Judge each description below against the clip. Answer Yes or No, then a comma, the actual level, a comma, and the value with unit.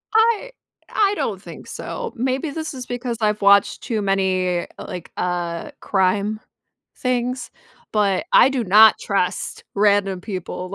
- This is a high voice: Yes, high, 210 Hz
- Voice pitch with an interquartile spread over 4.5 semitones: Yes, average, 5.0 semitones